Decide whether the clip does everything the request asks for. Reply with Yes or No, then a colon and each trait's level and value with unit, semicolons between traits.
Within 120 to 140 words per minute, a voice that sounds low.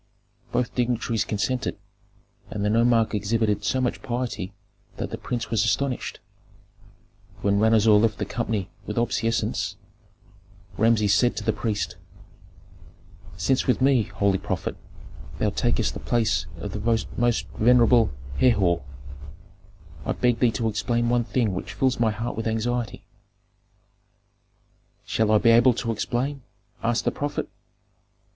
Yes: slow, 135 wpm; low, 115 Hz